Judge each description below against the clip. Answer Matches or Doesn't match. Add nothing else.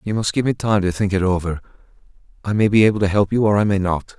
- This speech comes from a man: Matches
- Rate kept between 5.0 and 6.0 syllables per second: Doesn't match